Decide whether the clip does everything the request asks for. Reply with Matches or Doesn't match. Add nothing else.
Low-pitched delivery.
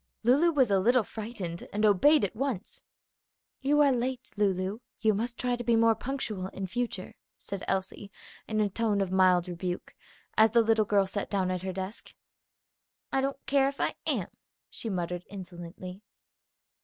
Doesn't match